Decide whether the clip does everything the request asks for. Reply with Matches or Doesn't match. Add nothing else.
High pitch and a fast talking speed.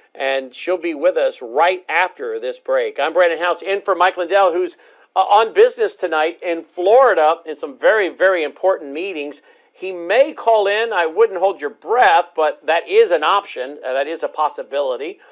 Doesn't match